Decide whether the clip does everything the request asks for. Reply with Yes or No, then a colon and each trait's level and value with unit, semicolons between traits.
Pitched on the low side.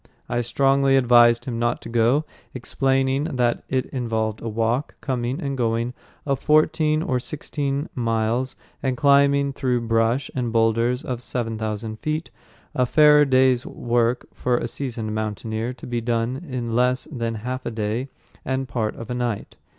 Yes: low, 125 Hz